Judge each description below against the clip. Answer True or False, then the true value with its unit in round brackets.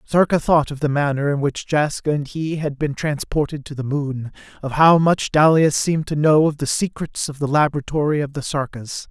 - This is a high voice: False (145 Hz)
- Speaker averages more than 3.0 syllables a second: True (5.2 syllables/s)